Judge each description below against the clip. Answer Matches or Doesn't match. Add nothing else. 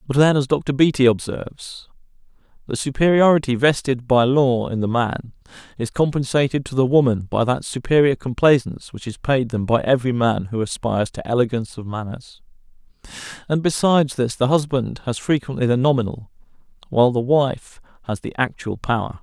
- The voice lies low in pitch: Matches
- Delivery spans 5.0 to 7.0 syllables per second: Matches